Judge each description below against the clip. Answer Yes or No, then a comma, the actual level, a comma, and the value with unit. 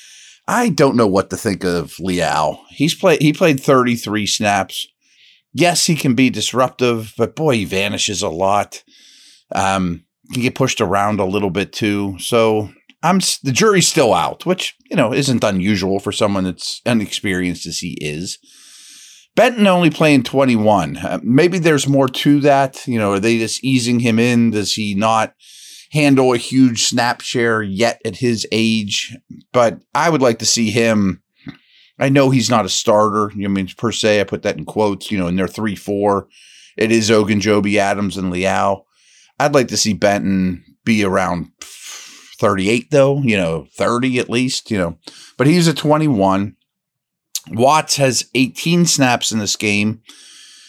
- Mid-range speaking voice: No, low, 110 Hz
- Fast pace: No, average, 170 wpm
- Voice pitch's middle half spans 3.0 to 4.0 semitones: No, average, 5.0 semitones